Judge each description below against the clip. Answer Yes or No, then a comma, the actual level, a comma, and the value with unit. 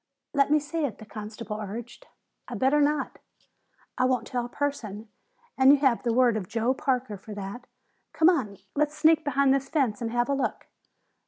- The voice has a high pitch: Yes, very high, 255 Hz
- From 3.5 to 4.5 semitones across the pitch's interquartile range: Yes, average, 4.2 semitones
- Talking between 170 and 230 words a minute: Yes, average, 190 wpm